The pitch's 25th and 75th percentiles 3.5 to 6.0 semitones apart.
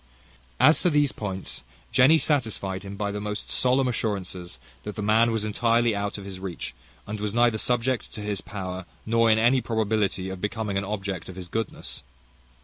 No: average, 2.9 semitones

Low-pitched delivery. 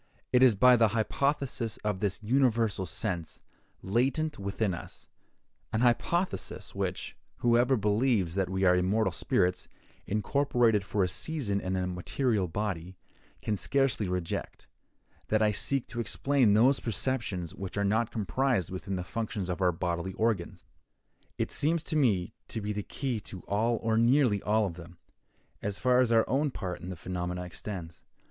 Yes: low, 105 Hz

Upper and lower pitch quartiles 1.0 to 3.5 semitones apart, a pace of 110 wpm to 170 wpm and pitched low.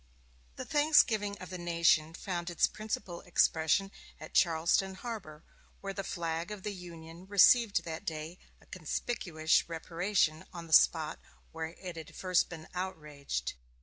No: average, 3.2 semitones; average, 145 wpm; medium, 175 Hz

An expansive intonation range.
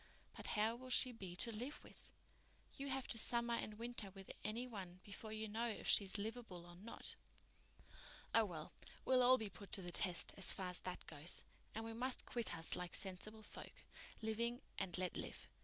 No: average, 4.1 semitones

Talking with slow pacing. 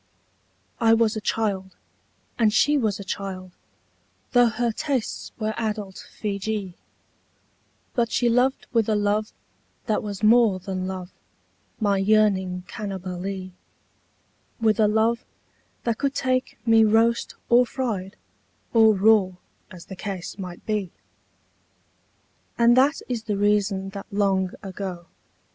Yes: slow, 130 wpm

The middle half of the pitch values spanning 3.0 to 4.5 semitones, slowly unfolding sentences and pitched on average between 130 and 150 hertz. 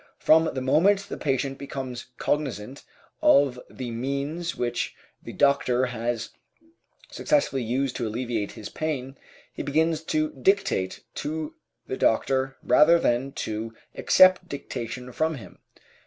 Yes: average, 4.2 semitones; slow, 125 wpm; low, 135 Hz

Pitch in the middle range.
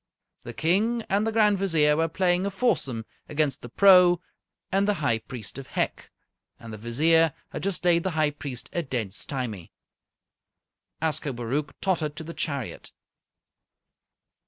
Yes: medium, 155 Hz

